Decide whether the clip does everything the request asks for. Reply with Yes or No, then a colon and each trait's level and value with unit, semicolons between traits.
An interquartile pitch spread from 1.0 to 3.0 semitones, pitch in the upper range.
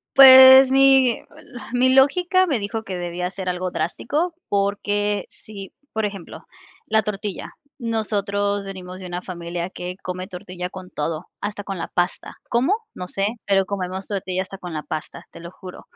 No: average, 3.6 semitones; high, 195 Hz